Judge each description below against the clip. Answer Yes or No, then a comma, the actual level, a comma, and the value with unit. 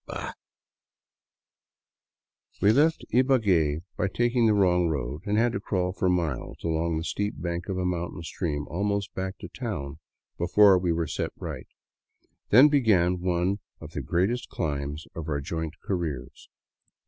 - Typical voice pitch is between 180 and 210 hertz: No, very low, 90 Hz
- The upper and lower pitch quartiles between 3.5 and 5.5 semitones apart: Yes, average, 4.0 semitones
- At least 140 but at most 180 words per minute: Yes, average, 155 wpm